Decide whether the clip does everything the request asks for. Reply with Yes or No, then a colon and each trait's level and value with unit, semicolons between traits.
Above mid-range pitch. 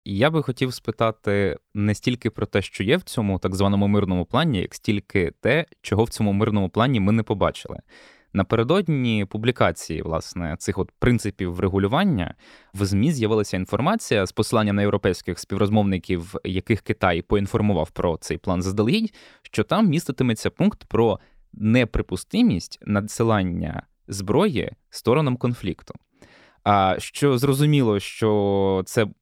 No: low, 105 Hz